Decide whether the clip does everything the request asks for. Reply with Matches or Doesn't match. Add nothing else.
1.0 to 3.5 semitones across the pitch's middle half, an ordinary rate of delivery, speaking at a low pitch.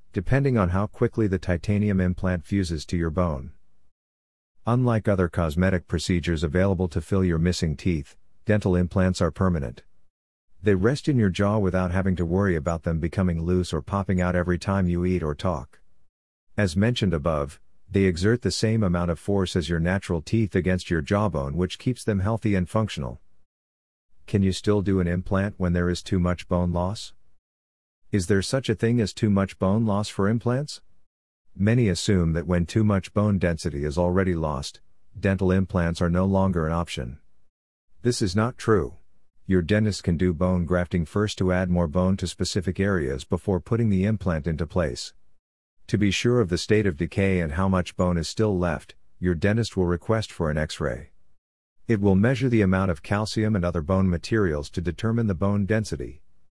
Matches